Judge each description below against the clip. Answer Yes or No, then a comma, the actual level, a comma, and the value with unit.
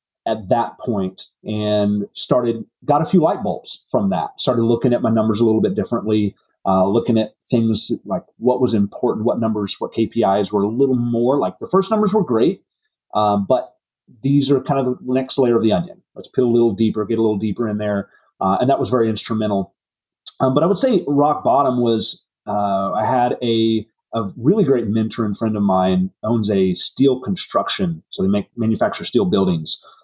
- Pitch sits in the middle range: No, low, 115 Hz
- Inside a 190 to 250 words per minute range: Yes, fast, 205 wpm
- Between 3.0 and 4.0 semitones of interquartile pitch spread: Yes, average, 3.6 semitones